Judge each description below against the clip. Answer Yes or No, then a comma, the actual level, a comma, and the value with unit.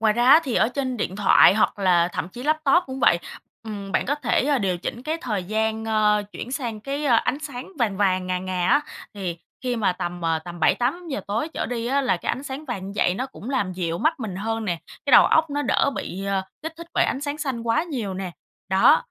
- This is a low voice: No, high, 225 Hz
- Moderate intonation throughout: No, wide, 6.2 semitones